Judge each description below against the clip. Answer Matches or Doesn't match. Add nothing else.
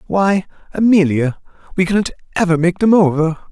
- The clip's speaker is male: Matches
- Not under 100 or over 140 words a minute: Matches